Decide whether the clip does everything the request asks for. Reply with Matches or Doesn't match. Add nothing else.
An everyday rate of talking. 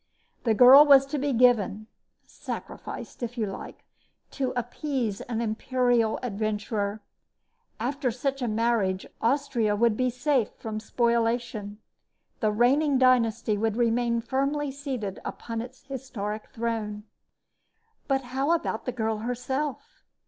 Doesn't match